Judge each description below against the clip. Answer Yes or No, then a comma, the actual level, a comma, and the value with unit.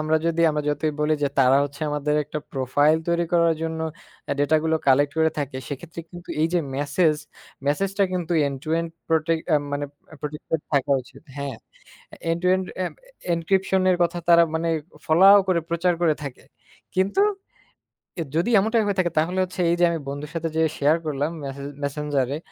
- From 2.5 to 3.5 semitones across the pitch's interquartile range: Yes, average, 3.0 semitones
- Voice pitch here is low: No, medium, 160 Hz